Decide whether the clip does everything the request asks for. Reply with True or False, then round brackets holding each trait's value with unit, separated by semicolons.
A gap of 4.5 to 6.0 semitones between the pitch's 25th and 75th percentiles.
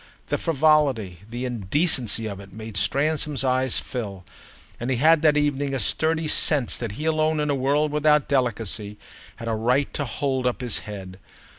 True (5.1 semitones)